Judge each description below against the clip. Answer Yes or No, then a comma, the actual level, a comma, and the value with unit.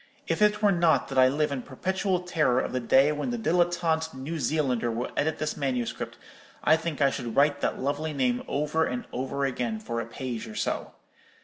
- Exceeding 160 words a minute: Yes, fast, 205 wpm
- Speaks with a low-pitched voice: No, medium, 145 Hz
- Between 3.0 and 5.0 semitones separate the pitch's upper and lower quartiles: Yes, average, 4.2 semitones